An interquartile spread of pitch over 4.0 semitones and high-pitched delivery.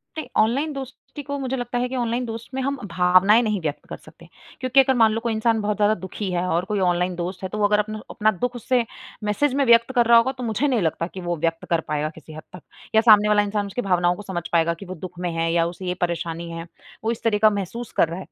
Yes: average, 5.1 semitones; high, 210 Hz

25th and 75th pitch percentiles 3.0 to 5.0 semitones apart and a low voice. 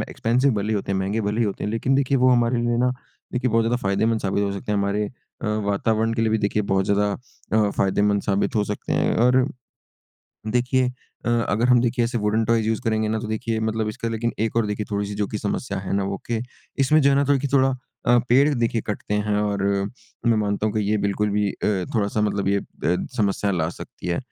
No: narrow, 2.6 semitones; low, 110 Hz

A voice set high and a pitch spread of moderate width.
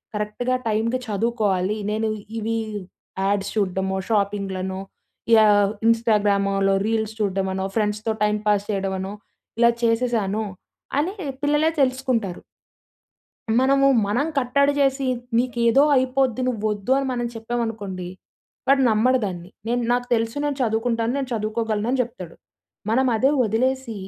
Yes: high, 225 Hz; average, 3.7 semitones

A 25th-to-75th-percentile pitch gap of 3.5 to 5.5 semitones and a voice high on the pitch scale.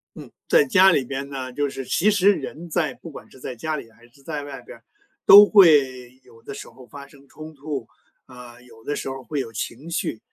No: average, 3.8 semitones; medium, 140 Hz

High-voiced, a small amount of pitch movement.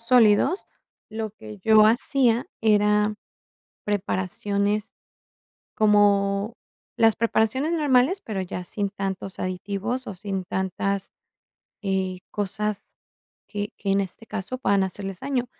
Yes: high, 205 Hz; narrow, 2.3 semitones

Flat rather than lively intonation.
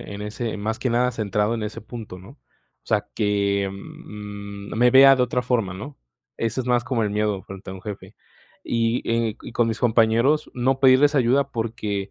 No: average, 3.2 semitones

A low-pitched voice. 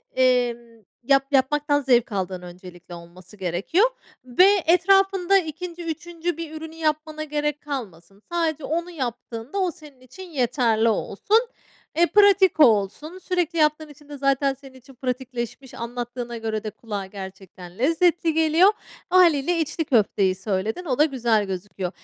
No: very high, 270 Hz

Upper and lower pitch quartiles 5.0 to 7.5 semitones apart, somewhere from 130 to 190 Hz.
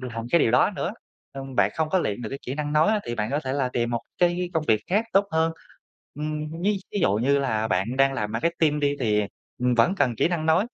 Yes: wide, 5.4 semitones; medium, 140 Hz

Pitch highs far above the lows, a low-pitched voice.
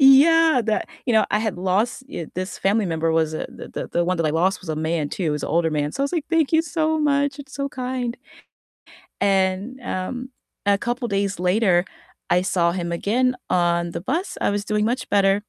No: wide, 6.8 semitones; high, 200 Hz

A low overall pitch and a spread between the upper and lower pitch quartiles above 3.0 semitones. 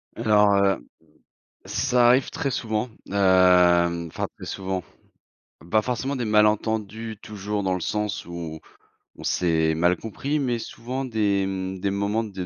Yes: low, 105 Hz; average, 3.4 semitones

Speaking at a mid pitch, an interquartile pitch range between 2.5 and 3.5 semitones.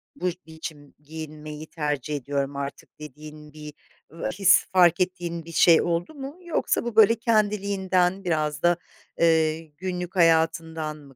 Yes: medium, 165 Hz; average, 3.2 semitones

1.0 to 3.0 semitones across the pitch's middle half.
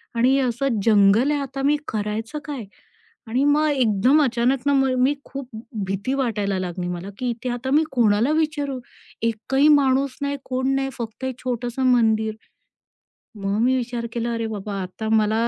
No: average, 3.7 semitones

